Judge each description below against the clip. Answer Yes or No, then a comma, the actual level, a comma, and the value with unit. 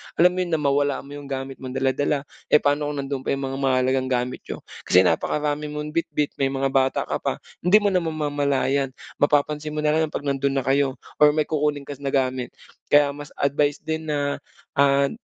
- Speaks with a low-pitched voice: No, medium, 145 Hz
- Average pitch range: No, narrow, 1.7 semitones